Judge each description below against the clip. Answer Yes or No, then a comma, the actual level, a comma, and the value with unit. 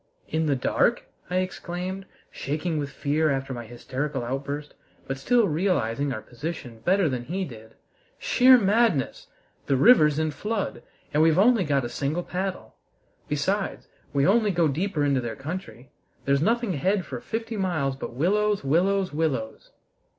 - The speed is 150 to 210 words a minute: Yes, average, 155 wpm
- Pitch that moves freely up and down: Yes, wide, 5.9 semitones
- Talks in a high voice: No, medium, 155 Hz